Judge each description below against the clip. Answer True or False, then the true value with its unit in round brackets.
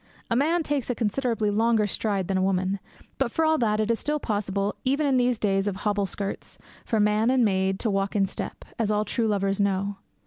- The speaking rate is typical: False (220 wpm)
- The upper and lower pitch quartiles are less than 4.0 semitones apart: True (3.4 semitones)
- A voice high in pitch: True (210 Hz)